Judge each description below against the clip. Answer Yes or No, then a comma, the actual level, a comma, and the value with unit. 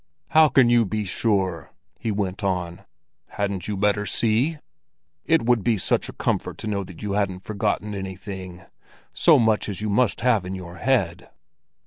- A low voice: Yes, low, 100 Hz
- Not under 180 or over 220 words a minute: No, average, 165 wpm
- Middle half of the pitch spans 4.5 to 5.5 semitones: No, average, 3.0 semitones